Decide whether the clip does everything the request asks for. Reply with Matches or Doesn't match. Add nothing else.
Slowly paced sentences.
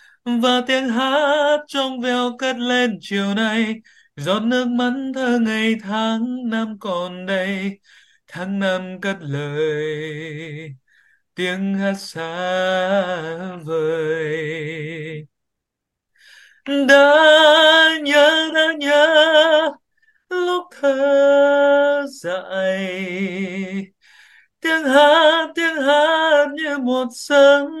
Matches